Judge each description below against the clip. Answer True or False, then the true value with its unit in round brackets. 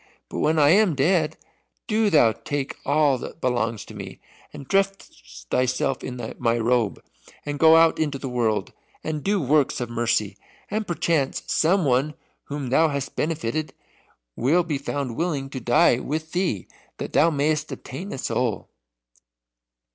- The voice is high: False (145 Hz)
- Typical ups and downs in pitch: True (4.4 semitones)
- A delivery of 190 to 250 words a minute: False (155 wpm)